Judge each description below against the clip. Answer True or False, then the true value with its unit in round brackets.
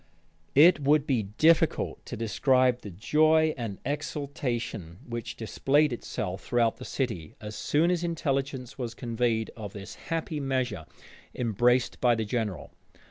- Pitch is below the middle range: True (125 Hz)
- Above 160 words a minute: False (135 wpm)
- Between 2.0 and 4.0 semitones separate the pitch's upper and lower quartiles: False (4.5 semitones)